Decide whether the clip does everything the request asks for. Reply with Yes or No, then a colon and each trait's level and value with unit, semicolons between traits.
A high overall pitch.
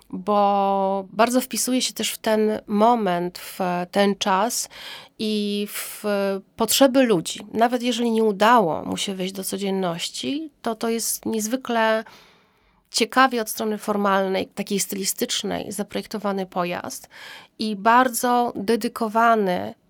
Yes: high, 220 Hz